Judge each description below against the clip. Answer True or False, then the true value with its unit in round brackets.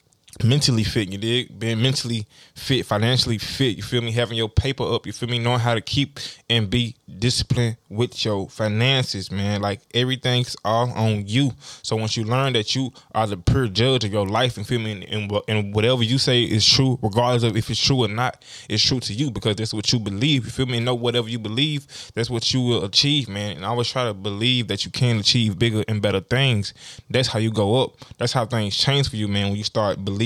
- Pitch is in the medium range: False (115 Hz)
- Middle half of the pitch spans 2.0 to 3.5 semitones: True (2.9 semitones)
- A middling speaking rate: False (240 wpm)